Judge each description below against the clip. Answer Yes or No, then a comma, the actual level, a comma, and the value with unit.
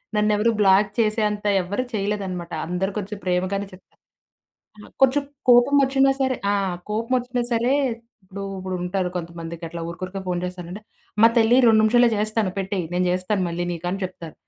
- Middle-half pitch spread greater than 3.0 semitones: Yes, average, 3.7 semitones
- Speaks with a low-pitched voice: No, high, 200 Hz